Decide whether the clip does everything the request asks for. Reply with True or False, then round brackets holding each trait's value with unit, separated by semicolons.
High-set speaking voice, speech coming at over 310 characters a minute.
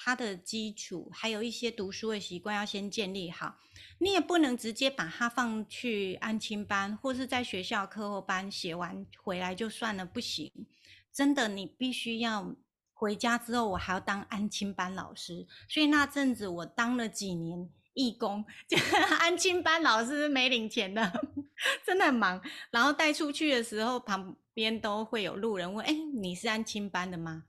False (220 Hz; 255 characters per minute)